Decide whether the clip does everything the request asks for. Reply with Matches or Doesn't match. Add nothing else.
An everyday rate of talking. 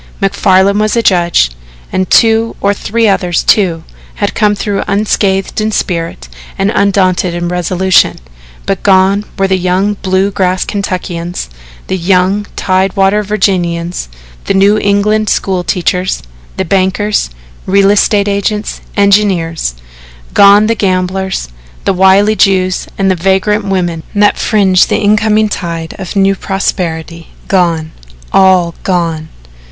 Doesn't match